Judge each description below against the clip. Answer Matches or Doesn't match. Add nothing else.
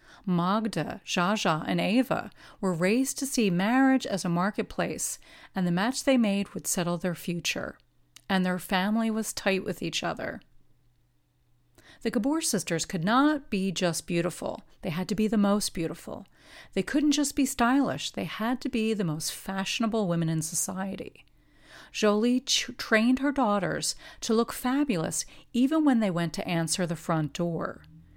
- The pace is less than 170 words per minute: Matches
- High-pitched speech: Matches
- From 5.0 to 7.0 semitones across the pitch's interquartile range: Matches